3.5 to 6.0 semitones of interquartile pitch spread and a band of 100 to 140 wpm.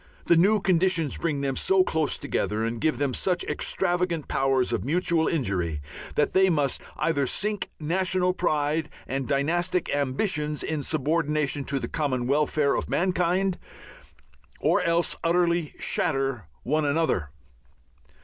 Yes: average, 4.0 semitones; slow, 135 wpm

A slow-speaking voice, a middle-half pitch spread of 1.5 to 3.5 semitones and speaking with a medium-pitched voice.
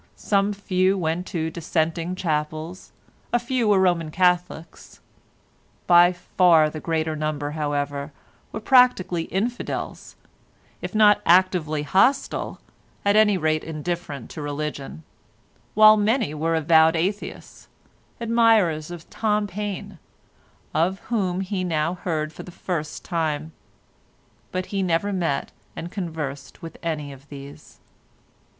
No: slow, 120 wpm; average, 4.0 semitones; medium, 170 Hz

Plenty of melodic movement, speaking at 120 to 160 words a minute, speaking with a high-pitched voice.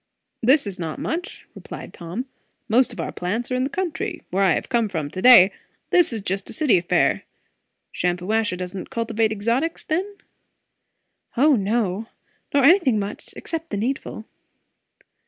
Yes: wide, 5.9 semitones; average, 155 wpm; high, 225 Hz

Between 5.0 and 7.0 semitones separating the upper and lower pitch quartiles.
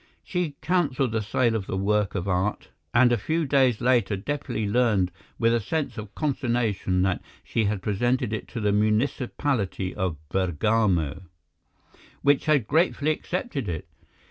Yes: average, 5.3 semitones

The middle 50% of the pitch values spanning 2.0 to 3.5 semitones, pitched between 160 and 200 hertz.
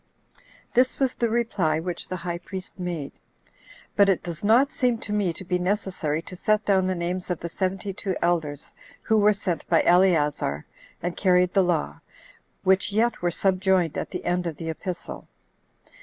Yes: average, 2.7 semitones; medium, 185 Hz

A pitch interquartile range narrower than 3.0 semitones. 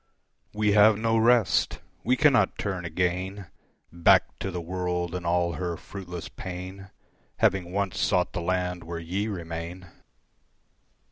Yes: narrow, 2.5 semitones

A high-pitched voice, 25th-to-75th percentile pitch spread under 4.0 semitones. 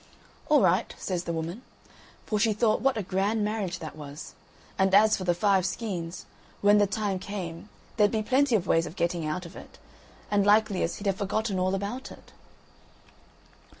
Yes: high, 195 Hz; average, 3.4 semitones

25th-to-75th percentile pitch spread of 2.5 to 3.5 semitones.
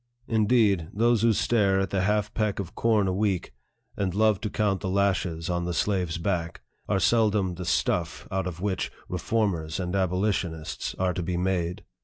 Yes: average, 2.9 semitones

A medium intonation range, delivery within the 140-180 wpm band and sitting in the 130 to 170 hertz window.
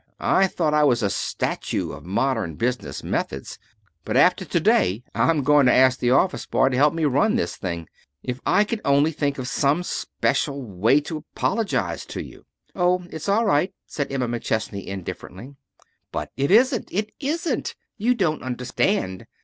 No: wide, 6.8 semitones; average, 175 wpm; medium, 140 Hz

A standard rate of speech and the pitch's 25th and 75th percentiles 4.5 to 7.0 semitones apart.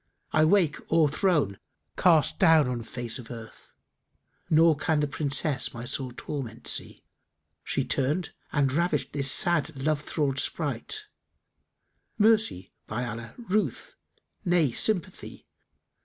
No: slow, 125 wpm; average, 4.8 semitones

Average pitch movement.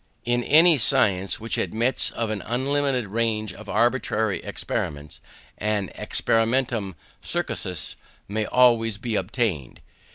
Yes: average, 3.1 semitones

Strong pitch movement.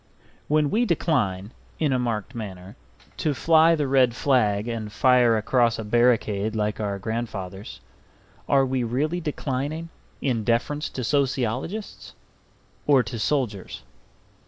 No: average, 4.9 semitones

